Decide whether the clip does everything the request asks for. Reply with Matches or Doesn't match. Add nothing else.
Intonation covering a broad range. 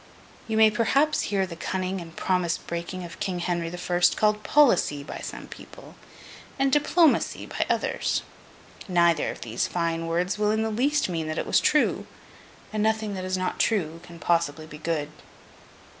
Doesn't match